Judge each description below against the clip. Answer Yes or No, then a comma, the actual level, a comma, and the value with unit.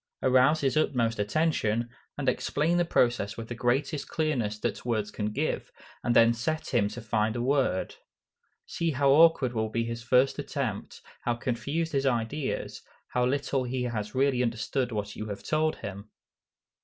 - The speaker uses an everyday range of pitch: Yes, average, 3.8 semitones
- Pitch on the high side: No, low, 125 Hz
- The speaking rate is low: No, average, 170 wpm